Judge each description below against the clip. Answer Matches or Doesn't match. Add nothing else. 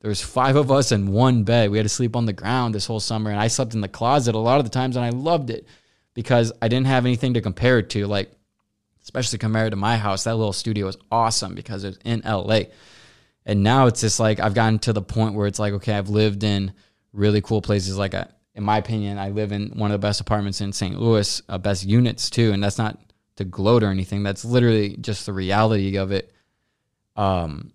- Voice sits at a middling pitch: Doesn't match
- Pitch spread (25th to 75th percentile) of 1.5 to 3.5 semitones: Matches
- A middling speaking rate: Doesn't match